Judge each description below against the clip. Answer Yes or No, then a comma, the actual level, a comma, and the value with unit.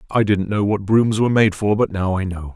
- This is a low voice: Yes, low, 100 Hz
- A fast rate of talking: Yes, fast, 280 wpm